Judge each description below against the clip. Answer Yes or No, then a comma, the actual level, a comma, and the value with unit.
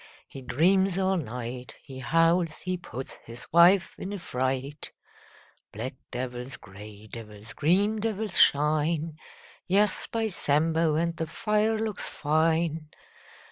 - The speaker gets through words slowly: Yes, slow, 130 wpm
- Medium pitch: Yes, medium, 160 Hz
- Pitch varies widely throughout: Yes, wide, 6.2 semitones